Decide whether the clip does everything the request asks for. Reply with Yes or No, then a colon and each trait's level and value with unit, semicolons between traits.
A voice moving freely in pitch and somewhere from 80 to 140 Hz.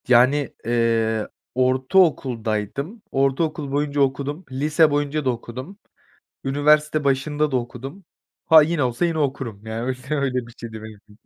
No: average, 3.9 semitones; low, 135 Hz